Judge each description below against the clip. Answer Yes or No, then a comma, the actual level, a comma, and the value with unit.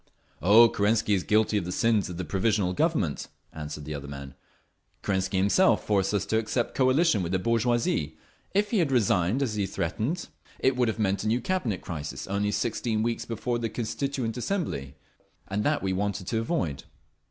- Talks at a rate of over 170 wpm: Yes, average, 185 wpm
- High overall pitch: No, low, 105 Hz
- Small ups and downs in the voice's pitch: No, average, 4.2 semitones